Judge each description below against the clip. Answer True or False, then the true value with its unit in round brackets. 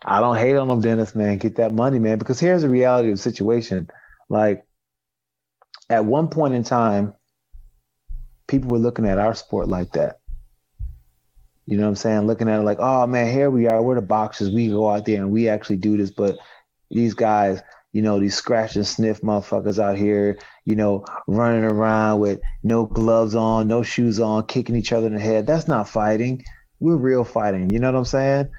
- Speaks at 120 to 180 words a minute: False (205 wpm)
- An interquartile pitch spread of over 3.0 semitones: False (2.7 semitones)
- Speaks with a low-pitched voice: True (110 Hz)